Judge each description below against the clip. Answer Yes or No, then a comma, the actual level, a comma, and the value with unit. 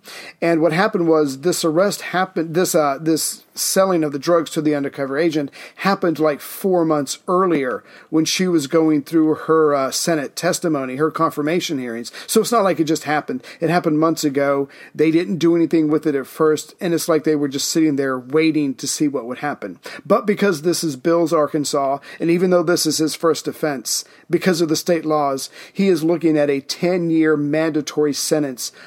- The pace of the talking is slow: No, average, 195 wpm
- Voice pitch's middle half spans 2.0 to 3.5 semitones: Yes, narrow, 2.6 semitones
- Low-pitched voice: No, medium, 160 Hz